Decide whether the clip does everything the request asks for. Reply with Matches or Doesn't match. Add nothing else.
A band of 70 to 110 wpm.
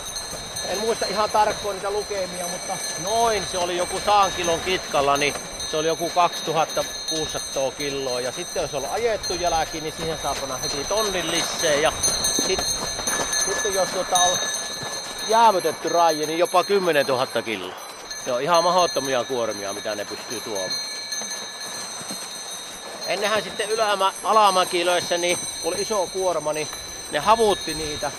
Doesn't match